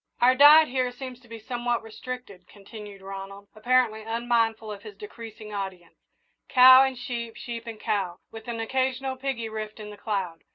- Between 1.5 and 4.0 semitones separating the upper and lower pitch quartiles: Yes, average, 3.1 semitones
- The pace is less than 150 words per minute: No, average, 170 wpm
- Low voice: No, high, 225 Hz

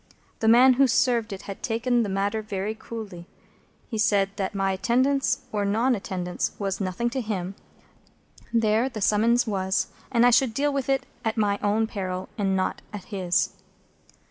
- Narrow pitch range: No, average, 3.5 semitones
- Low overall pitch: No, high, 215 Hz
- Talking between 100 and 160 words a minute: No, average, 175 wpm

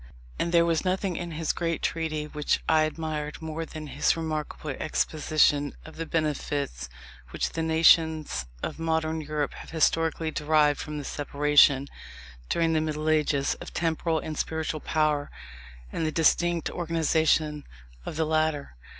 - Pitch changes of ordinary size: No, narrow, 1.4 semitones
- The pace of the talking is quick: No, average, 150 wpm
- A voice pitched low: No, medium, 155 Hz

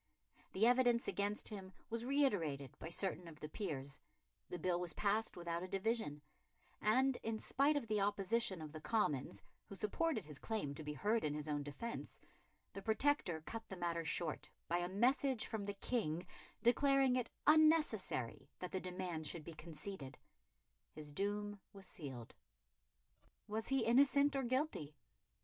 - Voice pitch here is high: Yes, high, 200 Hz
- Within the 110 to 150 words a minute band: No, average, 160 wpm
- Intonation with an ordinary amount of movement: No, wide, 6.7 semitones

